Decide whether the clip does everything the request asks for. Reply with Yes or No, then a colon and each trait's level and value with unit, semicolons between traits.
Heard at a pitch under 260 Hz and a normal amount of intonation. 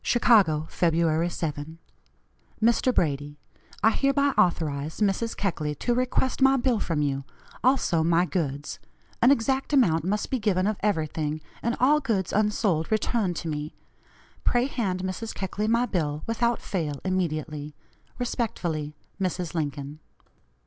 No: medium, 185 Hz; wide, 6.9 semitones